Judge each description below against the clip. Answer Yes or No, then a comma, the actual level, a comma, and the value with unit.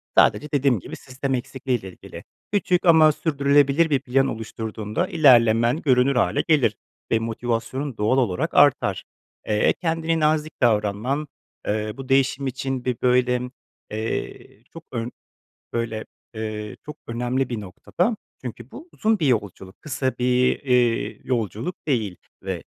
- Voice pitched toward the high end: No, low, 125 Hz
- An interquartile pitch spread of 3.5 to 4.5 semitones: Yes, average, 4.2 semitones